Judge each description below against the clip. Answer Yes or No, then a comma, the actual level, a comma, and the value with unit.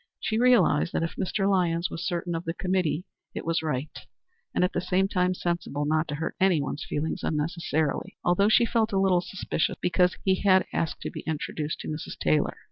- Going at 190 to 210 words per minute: Yes, average, 200 wpm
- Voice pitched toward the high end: No, medium, 175 Hz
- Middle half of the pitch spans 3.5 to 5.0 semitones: No, average, 3.0 semitones